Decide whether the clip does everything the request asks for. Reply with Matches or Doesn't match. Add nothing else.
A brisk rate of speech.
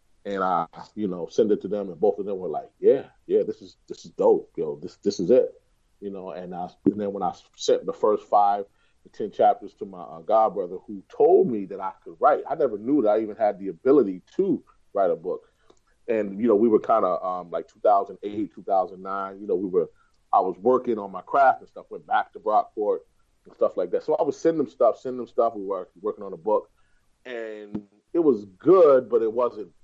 Matches